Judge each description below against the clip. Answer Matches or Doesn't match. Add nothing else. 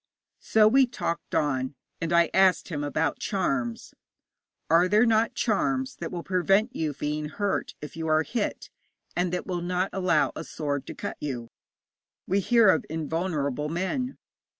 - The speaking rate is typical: Matches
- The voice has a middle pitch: Matches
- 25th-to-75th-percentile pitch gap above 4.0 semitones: Matches